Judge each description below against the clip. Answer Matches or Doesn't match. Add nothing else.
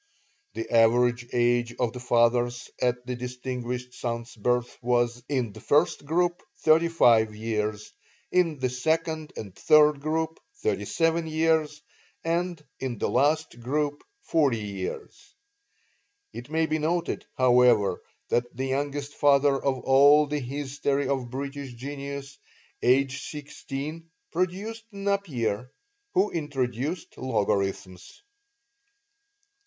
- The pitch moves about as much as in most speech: Matches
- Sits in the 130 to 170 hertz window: Matches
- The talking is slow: Matches